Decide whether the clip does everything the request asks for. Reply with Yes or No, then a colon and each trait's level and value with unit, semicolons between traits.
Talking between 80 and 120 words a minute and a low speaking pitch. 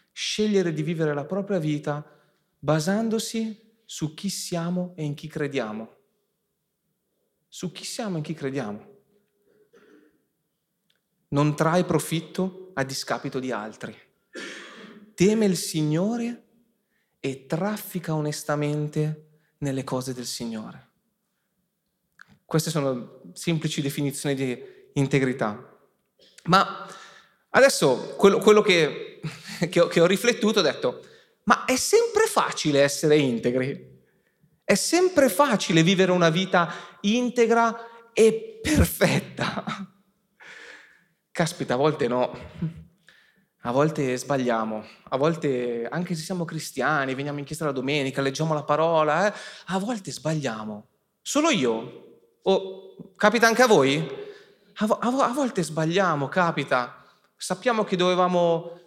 No: slow, 115 wpm; medium, 175 Hz